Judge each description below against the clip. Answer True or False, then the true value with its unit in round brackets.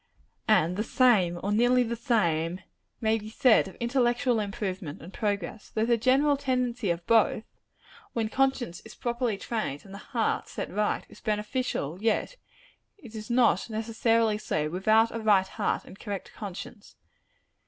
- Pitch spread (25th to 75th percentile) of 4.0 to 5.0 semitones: False (3.3 semitones)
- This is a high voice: True (220 Hz)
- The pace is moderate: True (155 wpm)